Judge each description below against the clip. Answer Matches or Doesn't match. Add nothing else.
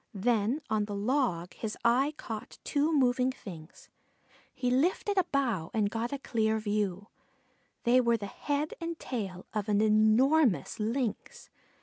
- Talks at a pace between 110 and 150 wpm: Matches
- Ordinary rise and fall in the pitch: Matches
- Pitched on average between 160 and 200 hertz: Doesn't match